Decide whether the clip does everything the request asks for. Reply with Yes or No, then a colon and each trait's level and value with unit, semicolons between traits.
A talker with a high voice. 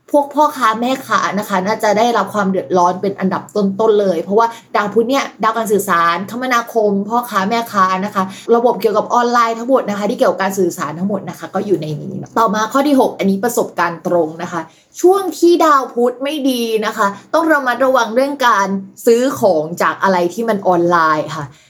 Yes: high, 215 Hz